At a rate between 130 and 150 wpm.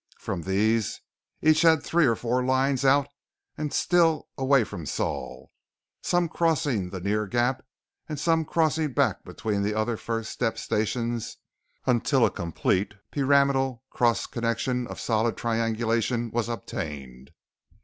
Yes: slow, 135 wpm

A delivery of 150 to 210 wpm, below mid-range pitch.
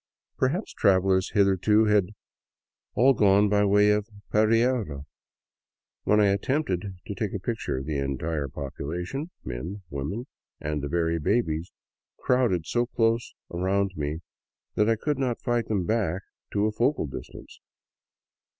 No: slow, 135 wpm; low, 100 Hz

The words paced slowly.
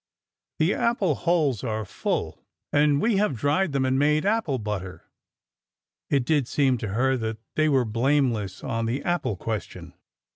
No: average, 155 wpm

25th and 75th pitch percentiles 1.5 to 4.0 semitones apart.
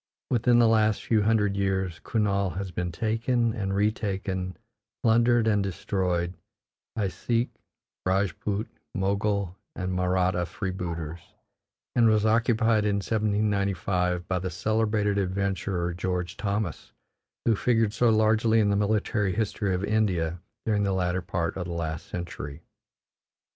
Yes: average, 3.1 semitones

